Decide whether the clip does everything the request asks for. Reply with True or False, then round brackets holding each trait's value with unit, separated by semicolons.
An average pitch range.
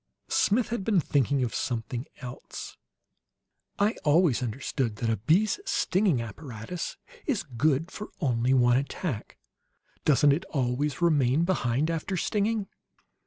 False (6.7 semitones)